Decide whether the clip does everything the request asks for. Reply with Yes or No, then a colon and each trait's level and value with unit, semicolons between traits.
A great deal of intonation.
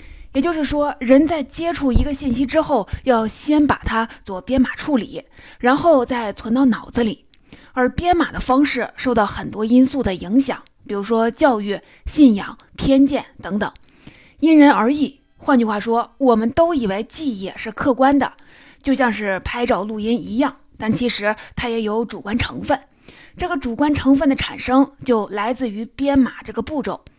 No: average, 3.6 semitones